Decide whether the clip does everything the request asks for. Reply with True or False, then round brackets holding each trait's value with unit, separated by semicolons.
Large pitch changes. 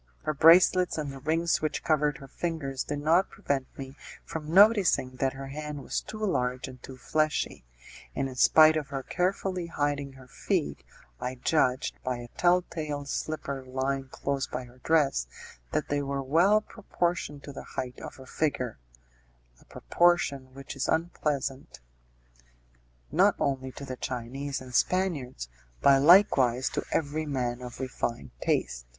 False (3.5 semitones)